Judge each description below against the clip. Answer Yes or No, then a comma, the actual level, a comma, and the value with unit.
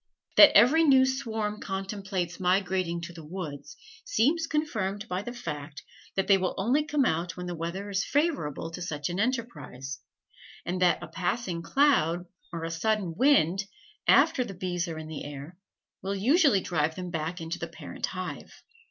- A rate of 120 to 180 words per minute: Yes, average, 170 wpm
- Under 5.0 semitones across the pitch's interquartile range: No, wide, 5.4 semitones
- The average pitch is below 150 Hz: No, medium, 185 Hz